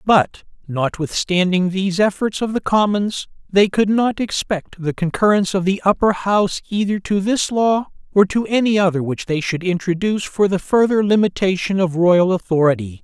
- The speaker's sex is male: Yes, male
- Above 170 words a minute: No, average, 165 wpm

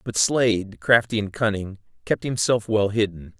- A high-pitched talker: No, low, 105 Hz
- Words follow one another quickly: No, average, 160 wpm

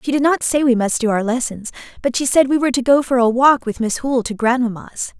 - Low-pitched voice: No, very high, 250 Hz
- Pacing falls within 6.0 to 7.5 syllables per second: Yes, 6.1 syllables/s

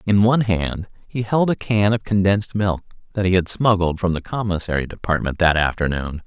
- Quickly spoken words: No, average, 190 wpm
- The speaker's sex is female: No, male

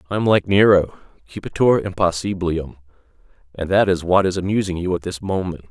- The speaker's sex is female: No, male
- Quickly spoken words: No, average, 160 wpm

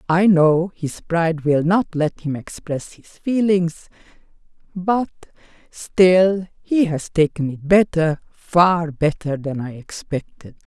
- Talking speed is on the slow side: Yes, slow, 130 wpm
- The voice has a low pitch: No, medium, 170 Hz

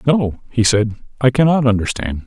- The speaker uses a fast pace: No, average, 160 wpm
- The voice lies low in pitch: Yes, low, 120 Hz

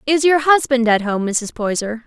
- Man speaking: No, female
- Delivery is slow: No, fast, 205 wpm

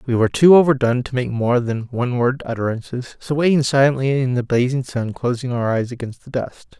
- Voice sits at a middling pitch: No, low, 125 Hz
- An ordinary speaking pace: No, fast, 210 wpm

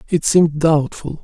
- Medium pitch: Yes, medium, 160 Hz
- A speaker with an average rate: Yes, average, 145 wpm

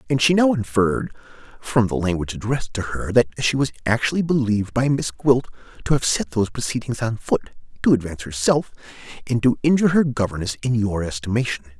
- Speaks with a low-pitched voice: Yes, low, 120 Hz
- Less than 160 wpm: No, average, 185 wpm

